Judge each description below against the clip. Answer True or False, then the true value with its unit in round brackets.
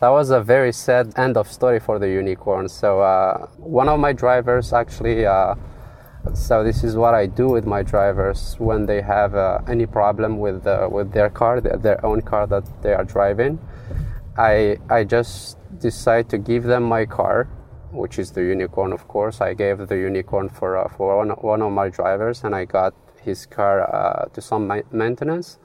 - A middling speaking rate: True (190 wpm)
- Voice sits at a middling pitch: False (110 Hz)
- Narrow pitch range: False (3.1 semitones)